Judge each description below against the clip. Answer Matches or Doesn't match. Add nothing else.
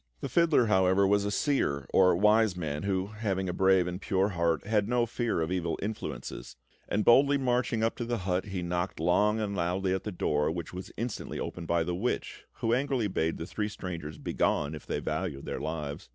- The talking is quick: Matches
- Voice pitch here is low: Matches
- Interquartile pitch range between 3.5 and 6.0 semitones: Matches